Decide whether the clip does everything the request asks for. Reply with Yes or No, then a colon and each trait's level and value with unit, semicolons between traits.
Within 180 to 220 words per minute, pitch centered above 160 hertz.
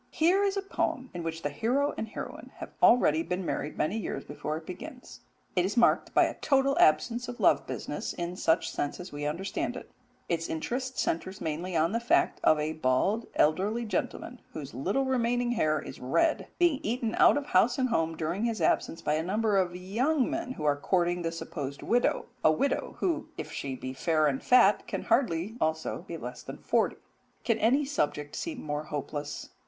Yes: average, 200 wpm; medium, 185 Hz